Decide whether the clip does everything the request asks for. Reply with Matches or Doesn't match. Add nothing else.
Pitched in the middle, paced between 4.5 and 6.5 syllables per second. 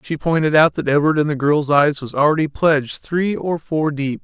Matches